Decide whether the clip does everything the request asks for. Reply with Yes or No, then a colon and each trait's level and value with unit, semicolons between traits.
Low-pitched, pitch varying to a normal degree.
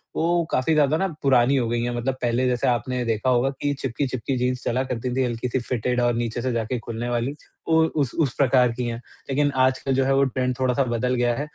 No: low, 125 Hz; narrow, 2.0 semitones